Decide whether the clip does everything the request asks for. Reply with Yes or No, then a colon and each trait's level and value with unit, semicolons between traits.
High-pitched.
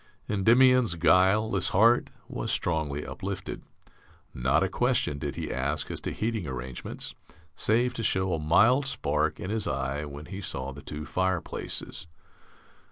No: very low, 85 Hz